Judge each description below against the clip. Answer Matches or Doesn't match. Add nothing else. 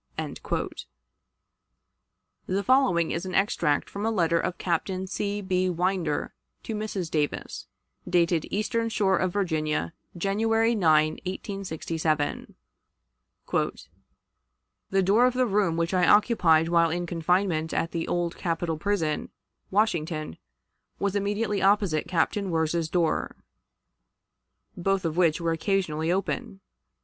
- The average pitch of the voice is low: Doesn't match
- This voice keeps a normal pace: Doesn't match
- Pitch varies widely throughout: Doesn't match